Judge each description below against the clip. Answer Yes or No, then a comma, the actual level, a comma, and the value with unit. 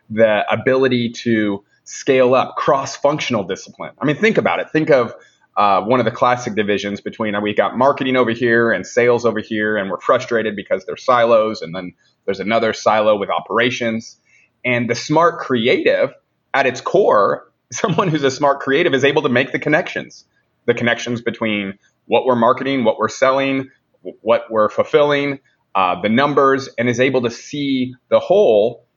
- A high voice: No, low, 120 Hz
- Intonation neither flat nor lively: Yes, average, 3.7 semitones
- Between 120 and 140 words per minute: No, average, 180 wpm